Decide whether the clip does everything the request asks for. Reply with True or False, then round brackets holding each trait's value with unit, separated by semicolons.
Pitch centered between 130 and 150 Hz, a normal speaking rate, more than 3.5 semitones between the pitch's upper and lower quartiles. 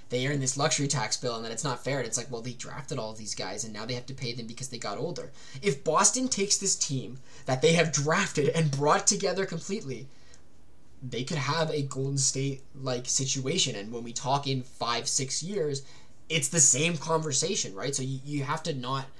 False (135 Hz; 220 wpm; 4.2 semitones)